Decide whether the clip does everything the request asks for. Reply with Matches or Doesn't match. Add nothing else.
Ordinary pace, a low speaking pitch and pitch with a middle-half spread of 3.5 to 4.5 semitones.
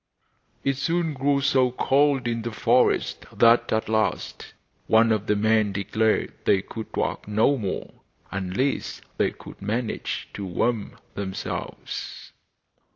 Doesn't match